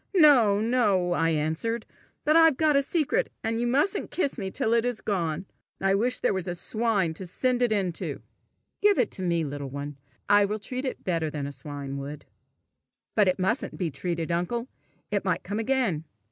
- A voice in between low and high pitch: No, high, 200 Hz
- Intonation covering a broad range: Yes, wide, 6.8 semitones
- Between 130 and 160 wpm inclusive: No, average, 195 wpm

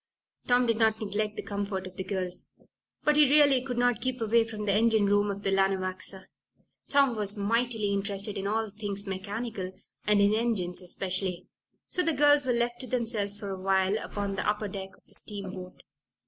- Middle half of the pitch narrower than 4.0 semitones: Yes, average, 3.2 semitones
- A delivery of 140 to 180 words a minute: No, average, 190 wpm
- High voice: Yes, high, 205 Hz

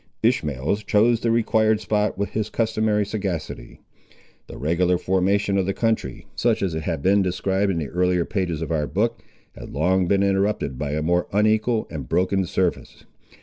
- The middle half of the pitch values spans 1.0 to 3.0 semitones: No, average, 3.8 semitones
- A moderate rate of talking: Yes, average, 175 wpm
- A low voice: Yes, very low, 95 Hz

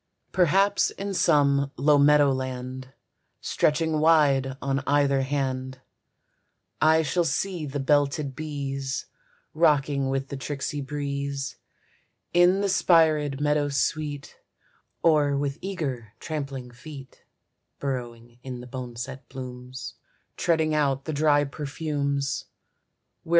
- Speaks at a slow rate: Yes, slow, 110 wpm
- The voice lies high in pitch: No, medium, 140 Hz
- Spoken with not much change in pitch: Yes, narrow, 2.3 semitones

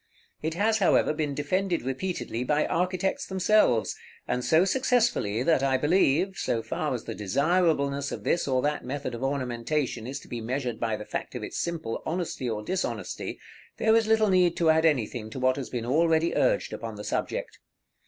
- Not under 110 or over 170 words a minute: No, average, 185 wpm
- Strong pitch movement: Yes, wide, 6.1 semitones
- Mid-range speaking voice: Yes, medium, 150 Hz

